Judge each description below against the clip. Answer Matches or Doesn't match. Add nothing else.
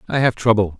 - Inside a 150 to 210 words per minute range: Doesn't match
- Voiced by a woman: Doesn't match